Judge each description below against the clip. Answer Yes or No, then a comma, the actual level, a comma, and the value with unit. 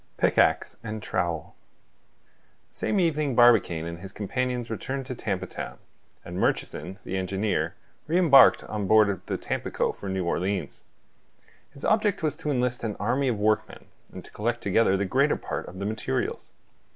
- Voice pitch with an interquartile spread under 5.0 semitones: No, average, 5.3 semitones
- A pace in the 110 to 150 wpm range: No, average, 165 wpm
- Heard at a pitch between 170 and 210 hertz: No, low, 110 Hz